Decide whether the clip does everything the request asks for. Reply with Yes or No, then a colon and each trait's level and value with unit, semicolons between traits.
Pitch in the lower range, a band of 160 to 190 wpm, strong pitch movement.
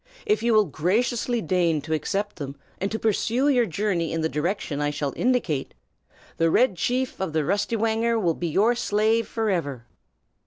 No: high, 200 Hz; average, 170 wpm; wide, 6.2 semitones